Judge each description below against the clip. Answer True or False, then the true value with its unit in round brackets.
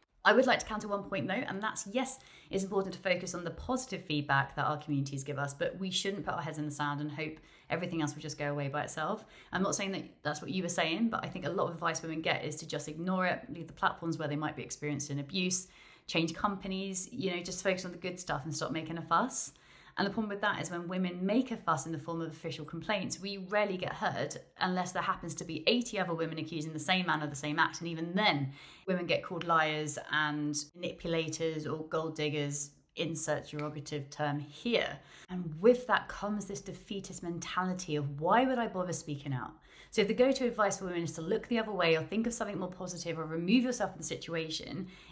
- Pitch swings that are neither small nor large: True (3.9 semitones)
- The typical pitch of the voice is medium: True (170 Hz)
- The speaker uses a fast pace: True (240 wpm)